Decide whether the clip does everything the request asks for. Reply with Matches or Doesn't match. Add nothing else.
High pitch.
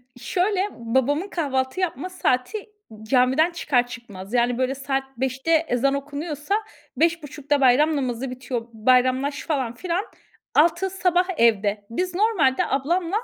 Matches